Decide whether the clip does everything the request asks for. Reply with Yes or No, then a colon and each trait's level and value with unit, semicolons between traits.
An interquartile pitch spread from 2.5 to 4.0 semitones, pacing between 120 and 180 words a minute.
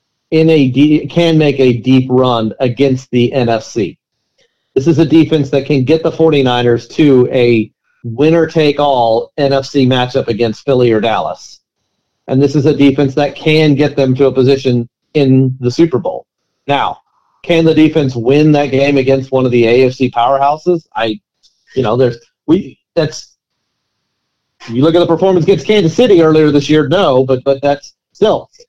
Yes: average, 3.4 semitones; average, 165 wpm